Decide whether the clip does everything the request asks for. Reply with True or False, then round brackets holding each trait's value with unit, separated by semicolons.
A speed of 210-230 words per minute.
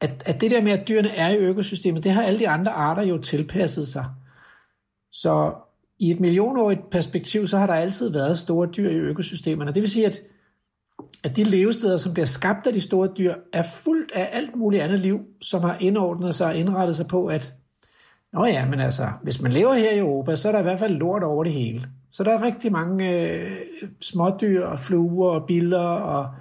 True (215 wpm)